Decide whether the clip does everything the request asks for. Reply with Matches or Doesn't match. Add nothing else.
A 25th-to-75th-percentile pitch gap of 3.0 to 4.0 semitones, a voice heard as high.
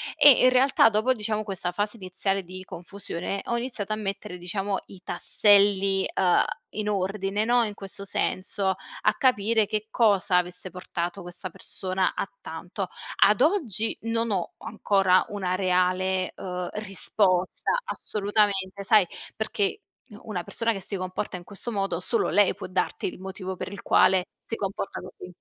Doesn't match